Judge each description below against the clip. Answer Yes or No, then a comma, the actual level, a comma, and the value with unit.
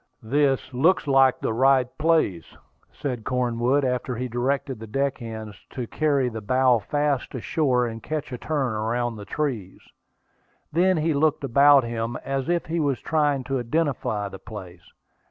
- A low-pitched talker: Yes, low, 130 Hz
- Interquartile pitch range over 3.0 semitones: Yes, average, 3.7 semitones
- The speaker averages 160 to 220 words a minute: Yes, average, 165 wpm